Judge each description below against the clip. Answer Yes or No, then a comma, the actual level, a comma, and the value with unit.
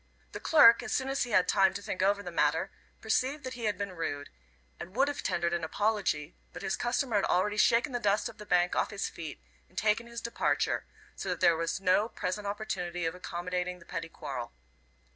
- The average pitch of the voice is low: No, high, 195 Hz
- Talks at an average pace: No, fast, 220 wpm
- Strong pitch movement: No, average, 4.1 semitones